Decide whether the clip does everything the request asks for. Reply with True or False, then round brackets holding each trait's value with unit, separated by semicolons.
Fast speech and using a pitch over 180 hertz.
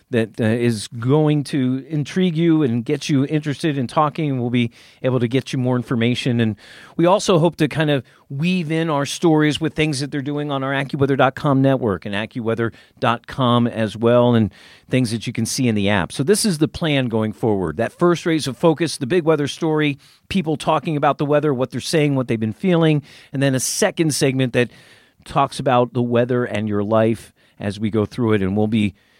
False (215 wpm; 135 Hz)